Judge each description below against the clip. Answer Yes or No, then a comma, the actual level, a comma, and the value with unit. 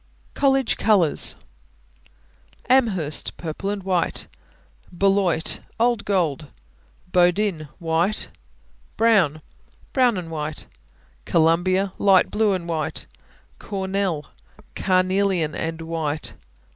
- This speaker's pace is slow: Yes, slow, 85 wpm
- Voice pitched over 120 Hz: Yes, medium, 185 Hz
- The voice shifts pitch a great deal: No, average, 3.7 semitones